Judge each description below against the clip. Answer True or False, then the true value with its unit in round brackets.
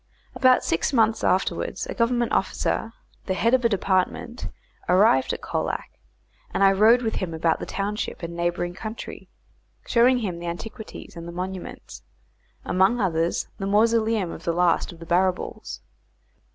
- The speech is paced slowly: False (155 wpm)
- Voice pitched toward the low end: False (195 Hz)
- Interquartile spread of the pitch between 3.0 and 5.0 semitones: True (4.7 semitones)